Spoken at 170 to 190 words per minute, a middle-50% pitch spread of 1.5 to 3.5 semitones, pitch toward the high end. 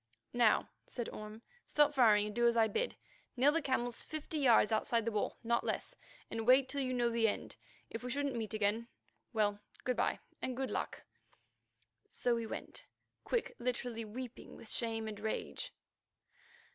Yes: average, 175 wpm; narrow, 2.6 semitones; high, 235 Hz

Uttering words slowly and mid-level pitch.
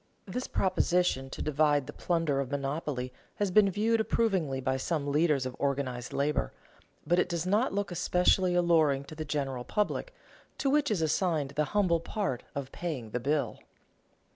No: average, 165 wpm; medium, 155 Hz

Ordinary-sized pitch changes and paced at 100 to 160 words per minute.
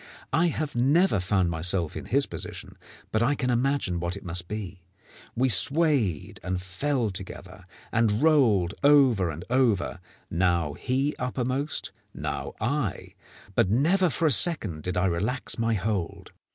No: wide, 7.2 semitones; average, 150 wpm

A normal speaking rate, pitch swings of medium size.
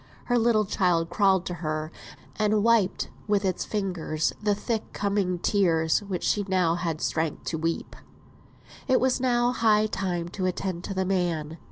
Yes: average, 165 wpm; average, 3.8 semitones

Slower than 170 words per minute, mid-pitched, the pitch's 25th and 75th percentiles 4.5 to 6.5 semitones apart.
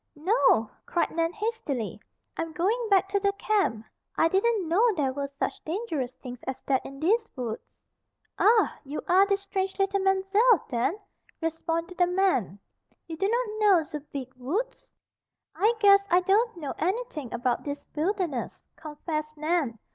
No: average, 155 wpm; very high, 350 Hz; wide, 5.5 semitones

